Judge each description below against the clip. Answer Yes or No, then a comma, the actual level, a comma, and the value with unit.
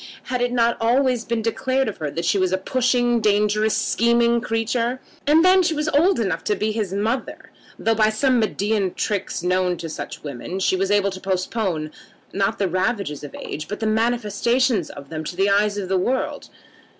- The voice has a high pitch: Yes, high, 215 Hz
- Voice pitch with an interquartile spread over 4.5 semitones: No, average, 4.1 semitones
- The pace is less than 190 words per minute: No, average, 200 wpm